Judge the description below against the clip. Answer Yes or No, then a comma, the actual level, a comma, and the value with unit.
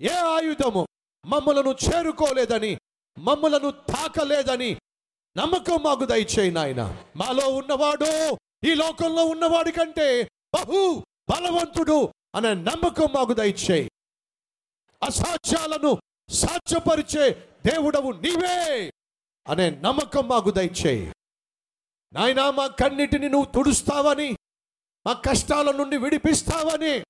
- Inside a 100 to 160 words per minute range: No, average, 80 wpm